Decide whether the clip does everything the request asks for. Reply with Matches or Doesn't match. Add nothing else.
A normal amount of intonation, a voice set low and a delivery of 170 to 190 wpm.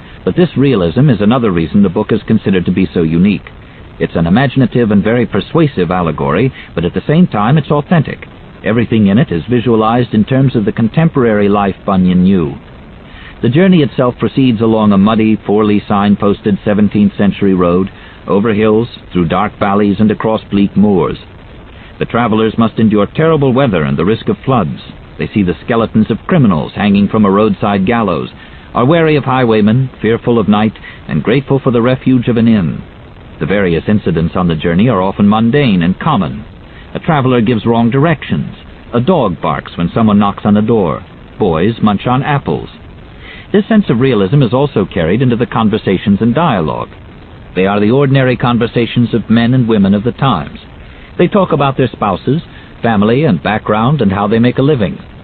Matches